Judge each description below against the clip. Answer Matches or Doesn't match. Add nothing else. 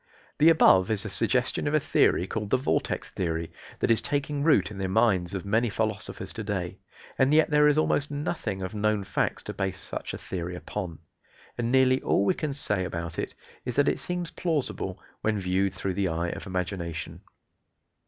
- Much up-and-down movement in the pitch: Matches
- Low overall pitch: Matches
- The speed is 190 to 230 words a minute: Matches